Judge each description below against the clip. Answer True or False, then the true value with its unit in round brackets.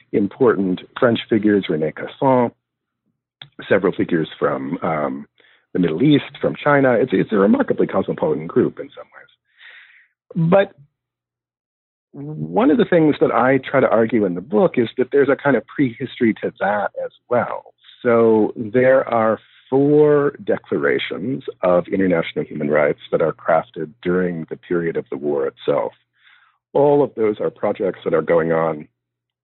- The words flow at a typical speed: True (155 wpm)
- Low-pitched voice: True (125 Hz)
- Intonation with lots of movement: True (6.3 semitones)